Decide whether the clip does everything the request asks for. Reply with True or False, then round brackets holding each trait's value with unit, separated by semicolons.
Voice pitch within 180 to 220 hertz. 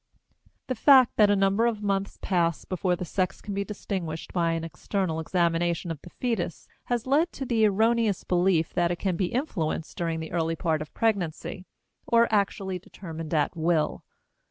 True (185 Hz)